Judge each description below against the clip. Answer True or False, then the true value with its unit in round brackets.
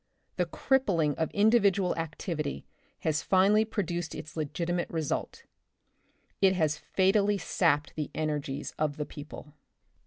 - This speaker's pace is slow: True (125 wpm)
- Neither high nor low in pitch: True (165 Hz)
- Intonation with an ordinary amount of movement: True (4.3 semitones)